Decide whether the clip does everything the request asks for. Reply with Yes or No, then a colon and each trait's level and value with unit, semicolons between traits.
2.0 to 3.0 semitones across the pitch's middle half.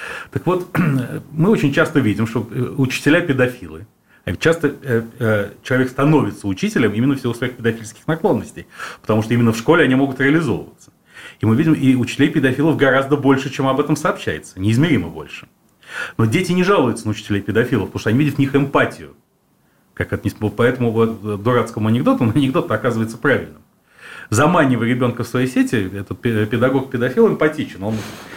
No: average, 4.2 semitones